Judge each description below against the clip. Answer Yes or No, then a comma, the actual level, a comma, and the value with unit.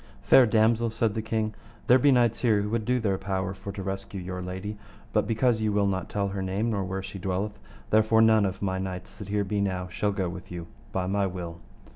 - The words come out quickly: Yes, fast, 230 wpm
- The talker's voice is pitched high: No, low, 100 Hz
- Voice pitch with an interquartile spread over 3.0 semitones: No, narrow, 2.6 semitones